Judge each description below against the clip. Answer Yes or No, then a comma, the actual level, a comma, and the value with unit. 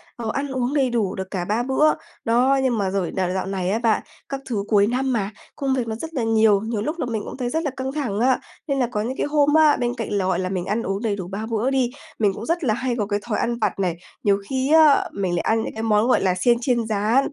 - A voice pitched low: No, high, 230 Hz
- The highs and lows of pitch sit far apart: No, average, 4.5 semitones